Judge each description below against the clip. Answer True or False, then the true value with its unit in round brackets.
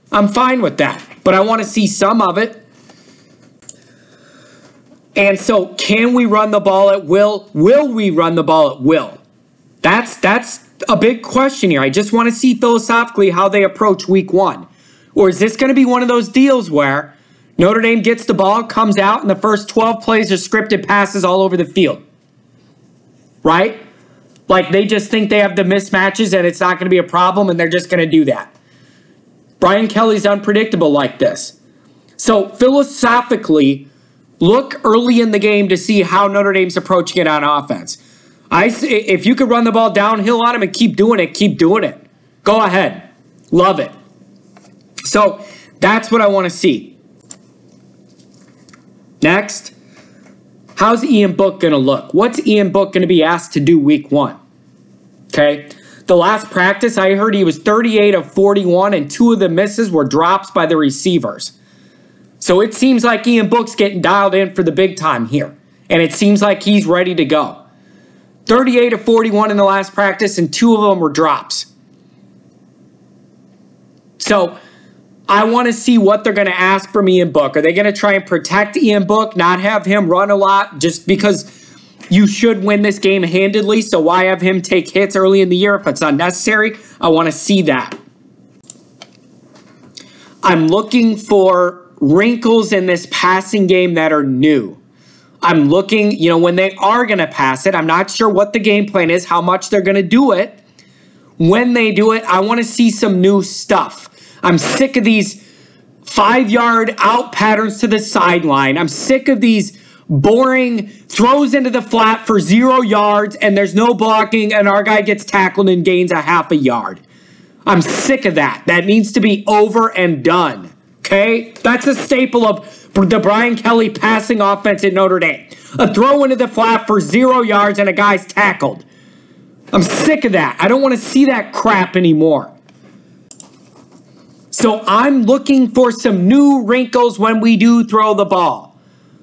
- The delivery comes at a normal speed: True (180 wpm)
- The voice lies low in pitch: False (200 Hz)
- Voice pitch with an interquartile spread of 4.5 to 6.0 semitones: False (3.9 semitones)